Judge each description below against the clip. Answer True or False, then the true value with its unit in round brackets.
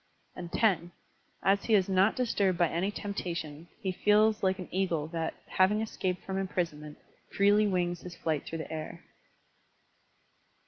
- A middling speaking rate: True (145 wpm)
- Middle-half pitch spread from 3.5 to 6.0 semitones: False (3.0 semitones)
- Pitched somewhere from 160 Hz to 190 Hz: True (185 Hz)